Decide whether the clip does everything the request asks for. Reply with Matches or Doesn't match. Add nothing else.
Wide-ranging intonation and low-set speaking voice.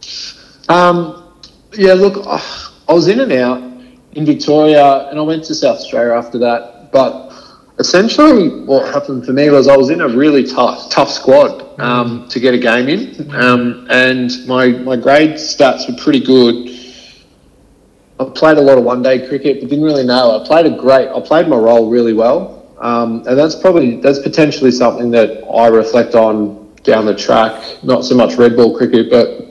Doesn't match